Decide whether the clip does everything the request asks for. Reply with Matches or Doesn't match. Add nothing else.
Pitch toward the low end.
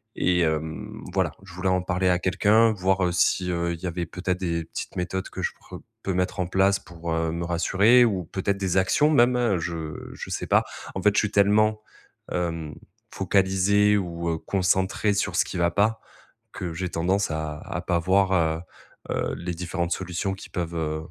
Matches